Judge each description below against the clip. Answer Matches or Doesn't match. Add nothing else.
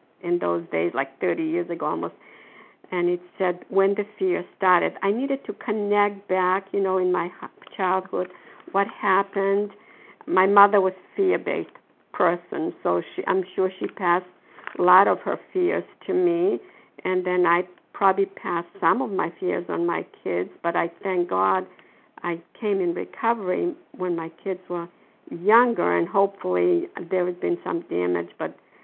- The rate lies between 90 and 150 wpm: Doesn't match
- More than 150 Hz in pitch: Matches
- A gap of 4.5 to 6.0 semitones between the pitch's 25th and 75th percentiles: Doesn't match